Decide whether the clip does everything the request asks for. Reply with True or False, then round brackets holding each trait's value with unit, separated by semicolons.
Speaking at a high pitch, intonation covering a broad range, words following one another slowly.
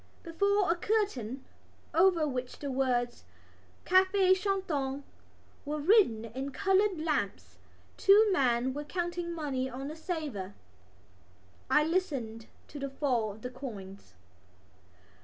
True (290 Hz; 6.6 semitones; 120 wpm)